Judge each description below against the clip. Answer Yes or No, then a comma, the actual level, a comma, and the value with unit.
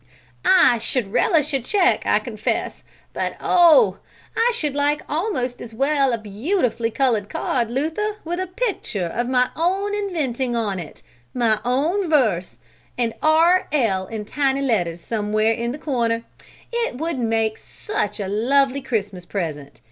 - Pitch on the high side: Yes, very high, 255 Hz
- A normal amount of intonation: No, wide, 6.4 semitones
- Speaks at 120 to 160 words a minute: Yes, average, 150 wpm